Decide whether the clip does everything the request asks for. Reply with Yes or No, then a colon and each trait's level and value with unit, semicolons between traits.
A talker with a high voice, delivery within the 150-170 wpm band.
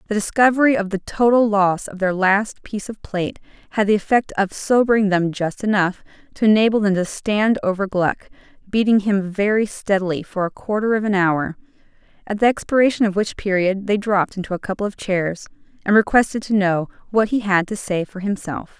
No: high, 200 Hz; average, 195 wpm